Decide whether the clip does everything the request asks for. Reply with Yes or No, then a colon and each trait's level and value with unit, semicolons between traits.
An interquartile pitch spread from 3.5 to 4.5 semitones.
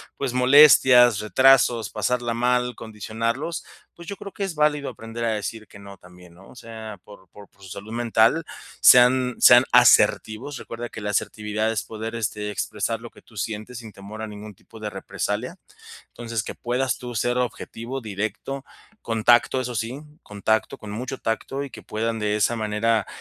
No: average, 2.7 semitones